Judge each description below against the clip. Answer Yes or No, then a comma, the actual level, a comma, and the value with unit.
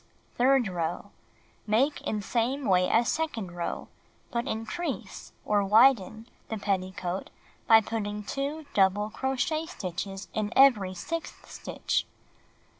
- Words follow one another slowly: Yes, slow, 115 wpm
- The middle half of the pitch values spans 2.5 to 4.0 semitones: No, wide, 5.4 semitones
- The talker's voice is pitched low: No, high, 220 Hz